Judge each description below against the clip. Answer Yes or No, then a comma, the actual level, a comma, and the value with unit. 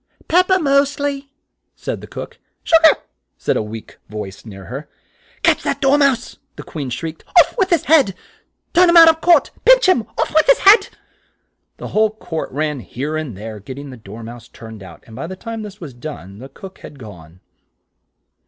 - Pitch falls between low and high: Yes, medium, 160 Hz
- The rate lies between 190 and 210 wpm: Yes, fast, 205 wpm